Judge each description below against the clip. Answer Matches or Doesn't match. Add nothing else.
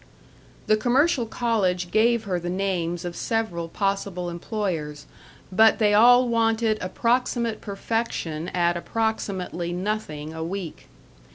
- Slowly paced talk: Matches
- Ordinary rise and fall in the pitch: Matches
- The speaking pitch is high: Matches